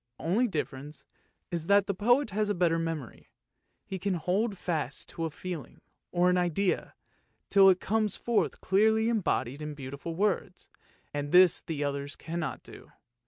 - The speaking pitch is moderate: Yes, medium, 180 Hz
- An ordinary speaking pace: Yes, average, 165 wpm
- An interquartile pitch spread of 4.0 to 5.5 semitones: Yes, average, 4.5 semitones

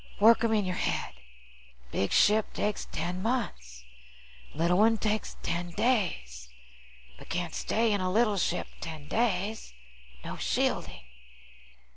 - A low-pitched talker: No, high, 195 Hz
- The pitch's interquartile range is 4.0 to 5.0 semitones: Yes, average, 4.4 semitones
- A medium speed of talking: No, slow, 130 wpm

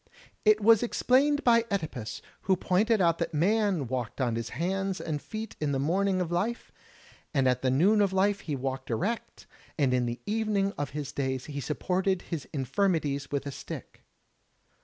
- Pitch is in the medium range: Yes, medium, 170 Hz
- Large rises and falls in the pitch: Yes, wide, 6.6 semitones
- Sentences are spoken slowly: No, average, 175 wpm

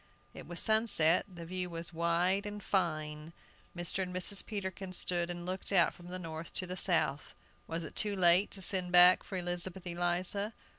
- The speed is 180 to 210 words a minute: Yes, average, 185 wpm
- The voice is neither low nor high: Yes, medium, 180 Hz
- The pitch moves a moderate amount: No, narrow, 1.7 semitones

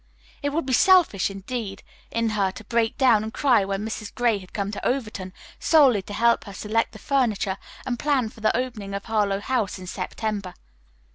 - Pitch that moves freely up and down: No, average, 3.7 semitones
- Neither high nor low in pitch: No, high, 220 Hz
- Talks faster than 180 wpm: Yes, average, 195 wpm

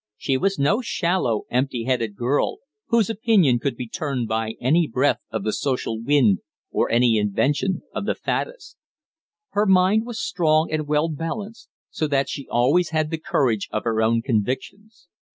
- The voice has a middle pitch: Yes, medium, 145 Hz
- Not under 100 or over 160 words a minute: No, average, 170 wpm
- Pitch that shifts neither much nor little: No, wide, 7.1 semitones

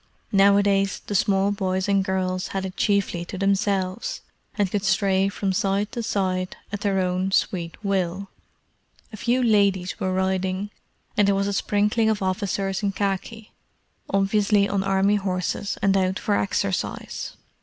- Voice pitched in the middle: No, high, 195 Hz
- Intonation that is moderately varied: No, narrow, 1.3 semitones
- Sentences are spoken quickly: No, average, 155 wpm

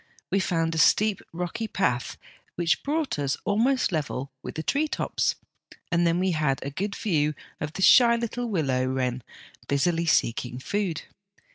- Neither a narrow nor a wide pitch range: No, wide, 6.5 semitones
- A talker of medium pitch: Yes, medium, 170 Hz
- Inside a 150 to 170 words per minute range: Yes, average, 160 wpm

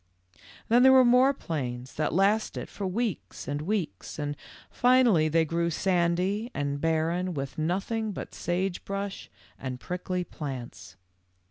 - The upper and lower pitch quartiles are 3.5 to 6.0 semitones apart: Yes, average, 5.2 semitones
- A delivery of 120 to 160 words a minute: Yes, slow, 135 wpm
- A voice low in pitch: No, medium, 175 Hz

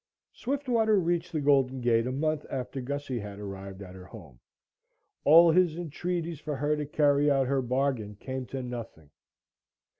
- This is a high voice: No, low, 135 Hz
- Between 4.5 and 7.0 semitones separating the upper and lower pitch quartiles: Yes, average, 4.9 semitones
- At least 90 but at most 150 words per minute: No, average, 160 wpm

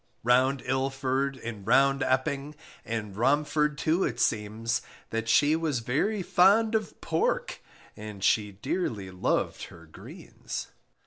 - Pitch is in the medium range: No, low, 130 Hz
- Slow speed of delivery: Yes, slow, 125 wpm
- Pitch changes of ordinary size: Yes, average, 5.0 semitones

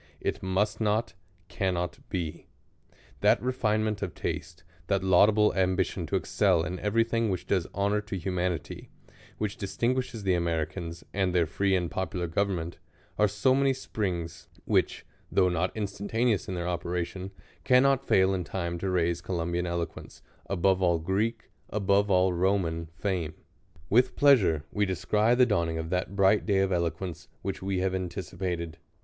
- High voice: No, very low, 95 Hz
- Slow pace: No, average, 155 wpm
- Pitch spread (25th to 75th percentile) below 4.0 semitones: Yes, average, 3.1 semitones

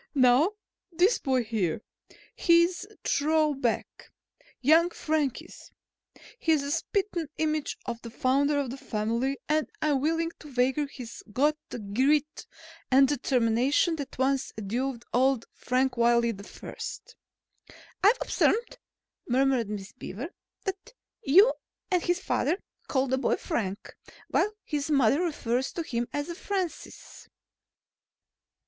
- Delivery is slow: Yes, slow, 130 wpm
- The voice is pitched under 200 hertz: No, very high, 275 Hz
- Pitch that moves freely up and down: No, average, 4.6 semitones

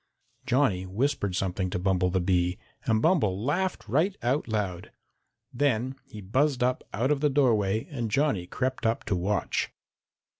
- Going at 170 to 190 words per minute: No, average, 155 wpm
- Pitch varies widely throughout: Yes, wide, 6.3 semitones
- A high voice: No, low, 110 Hz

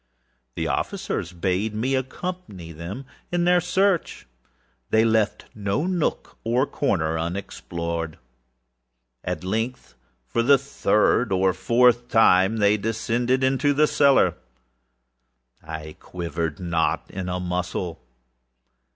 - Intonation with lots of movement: Yes, wide, 6.7 semitones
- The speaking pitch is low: Yes, low, 105 Hz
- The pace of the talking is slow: Yes, slow, 110 wpm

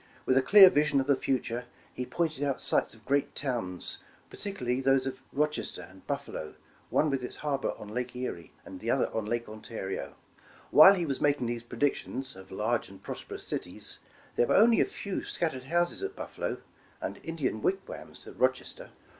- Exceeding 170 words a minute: Yes, average, 180 wpm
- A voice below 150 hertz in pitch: Yes, low, 135 Hz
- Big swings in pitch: No, average, 4.2 semitones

